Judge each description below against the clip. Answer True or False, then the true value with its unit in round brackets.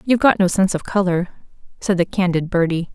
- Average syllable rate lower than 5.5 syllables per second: False (6.2 syllables/s)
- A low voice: False (185 Hz)